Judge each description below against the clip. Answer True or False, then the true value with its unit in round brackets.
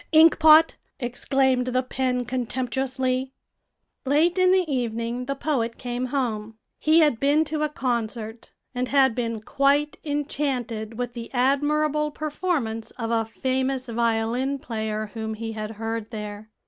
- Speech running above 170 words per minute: False (135 wpm)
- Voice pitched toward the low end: False (255 Hz)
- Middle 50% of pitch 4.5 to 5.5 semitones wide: False (3.8 semitones)